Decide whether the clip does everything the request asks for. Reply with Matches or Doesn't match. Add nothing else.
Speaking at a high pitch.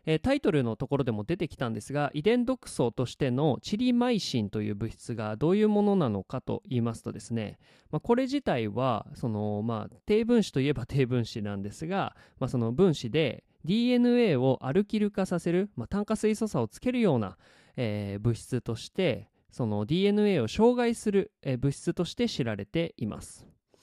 Doesn't match